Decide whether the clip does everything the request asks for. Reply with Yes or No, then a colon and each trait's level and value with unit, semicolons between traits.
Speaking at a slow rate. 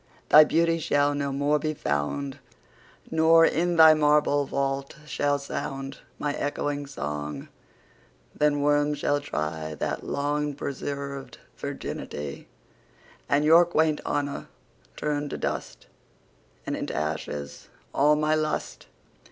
Yes: slow, 105 wpm